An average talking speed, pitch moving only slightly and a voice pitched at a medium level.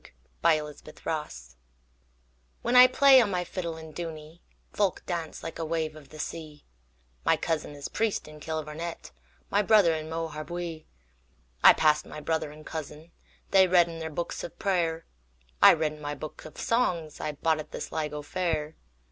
Yes: average, 155 wpm; narrow, 2.2 semitones; medium, 155 Hz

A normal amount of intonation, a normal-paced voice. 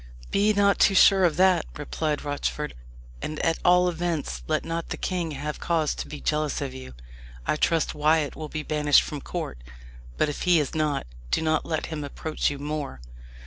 No: narrow, 2.2 semitones; average, 190 wpm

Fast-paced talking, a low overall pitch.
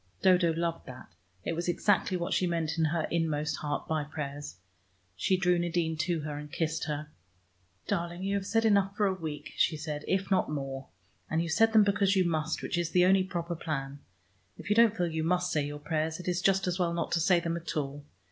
No: fast, 225 wpm; medium, 170 Hz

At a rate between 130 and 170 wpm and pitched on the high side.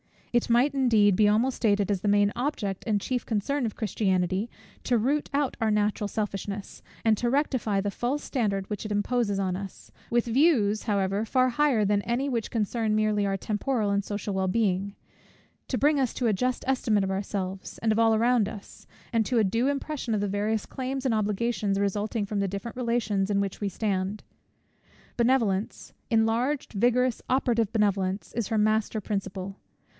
No: average, 180 wpm; high, 215 Hz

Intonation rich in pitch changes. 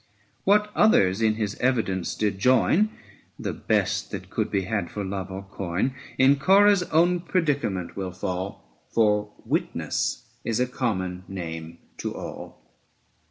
Yes: wide, 6.2 semitones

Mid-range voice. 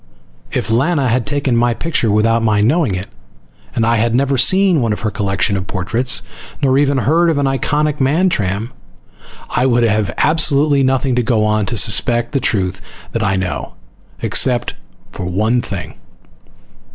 No: low, 120 Hz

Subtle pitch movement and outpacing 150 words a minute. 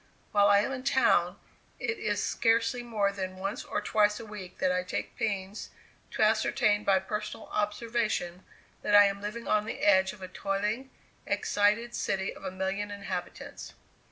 Yes: narrow, 2.3 semitones; average, 170 wpm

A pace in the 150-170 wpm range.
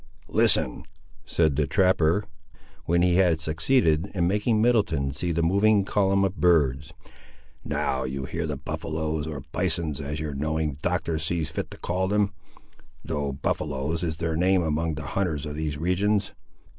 Yes: average, 160 wpm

